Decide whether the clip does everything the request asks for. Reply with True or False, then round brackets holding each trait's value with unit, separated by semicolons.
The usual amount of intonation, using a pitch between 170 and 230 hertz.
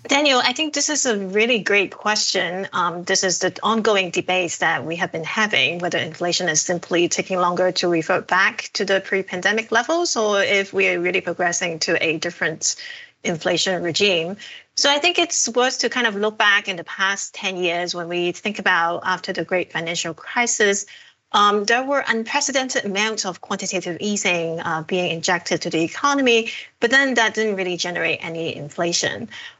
True (4.3 semitones; 190 Hz)